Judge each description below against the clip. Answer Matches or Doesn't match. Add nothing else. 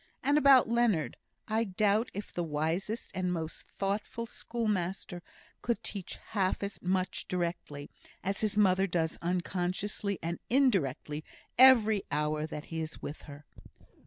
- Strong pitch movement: Doesn't match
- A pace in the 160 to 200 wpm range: Doesn't match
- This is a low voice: Doesn't match